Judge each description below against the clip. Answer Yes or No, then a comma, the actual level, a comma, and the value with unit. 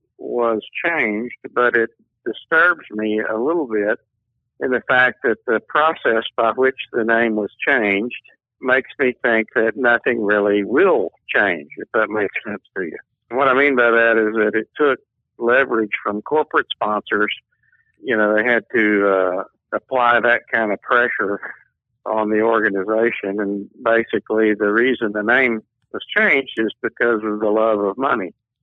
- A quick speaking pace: No, average, 165 wpm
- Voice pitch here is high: No, low, 110 Hz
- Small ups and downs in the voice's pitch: Yes, narrow, 1.9 semitones